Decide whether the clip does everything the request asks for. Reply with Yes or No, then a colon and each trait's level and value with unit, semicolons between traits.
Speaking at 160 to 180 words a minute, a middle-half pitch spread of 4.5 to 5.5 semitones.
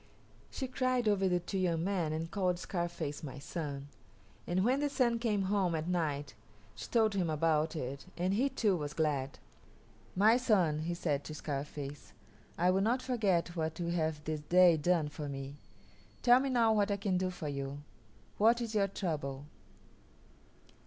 Yes: average, 175 wpm; average, 5.1 semitones